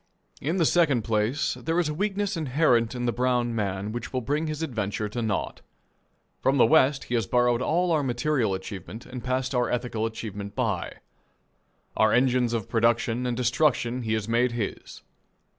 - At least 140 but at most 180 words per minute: Yes, average, 175 wpm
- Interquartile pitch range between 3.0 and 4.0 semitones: Yes, average, 3.6 semitones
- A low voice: Yes, low, 120 Hz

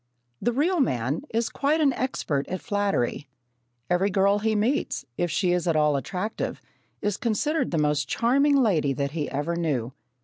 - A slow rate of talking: No, average, 170 wpm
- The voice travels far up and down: Yes, wide, 7.8 semitones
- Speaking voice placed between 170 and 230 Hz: Yes, medium, 185 Hz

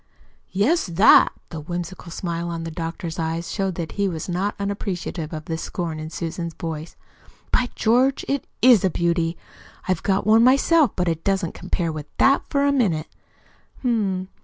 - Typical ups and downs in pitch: Yes, average, 4.0 semitones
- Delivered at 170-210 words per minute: Yes, average, 175 wpm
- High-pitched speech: No, medium, 180 Hz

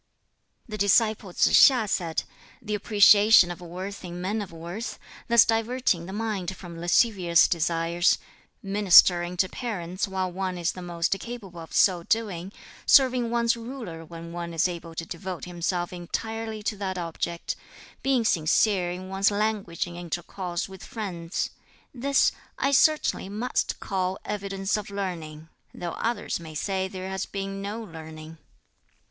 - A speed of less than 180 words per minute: Yes, average, 150 wpm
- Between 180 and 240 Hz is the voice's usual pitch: Yes, high, 190 Hz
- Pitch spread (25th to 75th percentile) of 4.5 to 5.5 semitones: No, average, 3.6 semitones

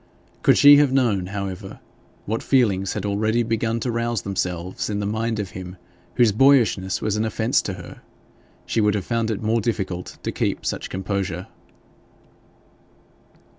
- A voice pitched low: Yes, low, 105 Hz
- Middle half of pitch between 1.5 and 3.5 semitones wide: Yes, average, 3.2 semitones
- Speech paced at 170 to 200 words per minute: No, average, 160 wpm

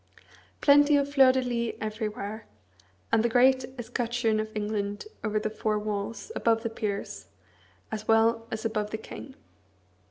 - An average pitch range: No, narrow, 2.3 semitones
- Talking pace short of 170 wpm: Yes, average, 150 wpm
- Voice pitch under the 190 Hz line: No, high, 225 Hz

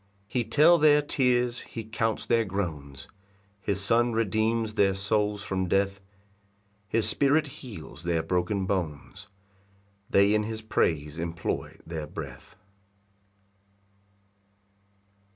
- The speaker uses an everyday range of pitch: Yes, average, 4.0 semitones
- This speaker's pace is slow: Yes, slow, 115 wpm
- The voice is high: No, low, 100 Hz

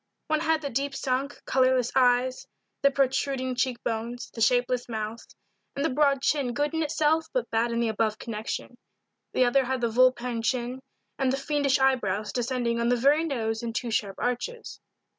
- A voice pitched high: Yes, very high, 255 Hz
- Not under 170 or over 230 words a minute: Yes, average, 180 wpm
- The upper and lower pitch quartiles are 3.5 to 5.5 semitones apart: No, average, 2.9 semitones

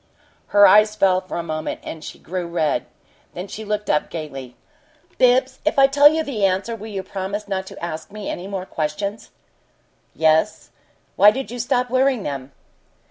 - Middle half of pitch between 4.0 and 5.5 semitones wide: Yes, average, 5.2 semitones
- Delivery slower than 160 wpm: No, average, 175 wpm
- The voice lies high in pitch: Yes, high, 200 Hz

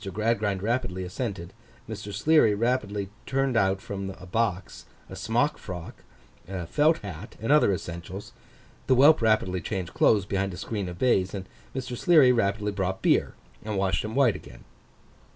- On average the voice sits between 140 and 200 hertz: No, low, 105 Hz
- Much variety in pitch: No, average, 4.1 semitones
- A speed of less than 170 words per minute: Yes, average, 155 wpm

